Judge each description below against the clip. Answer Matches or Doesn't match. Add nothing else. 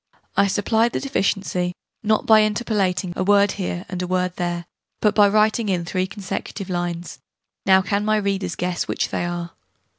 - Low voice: Doesn't match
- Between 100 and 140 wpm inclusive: Doesn't match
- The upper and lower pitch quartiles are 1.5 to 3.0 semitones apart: Matches